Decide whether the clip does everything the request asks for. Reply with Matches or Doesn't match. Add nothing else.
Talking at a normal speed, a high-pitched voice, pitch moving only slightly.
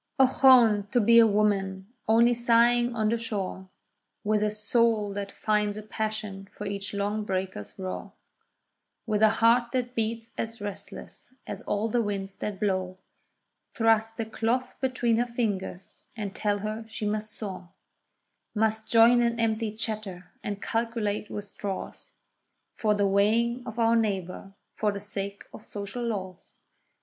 Matches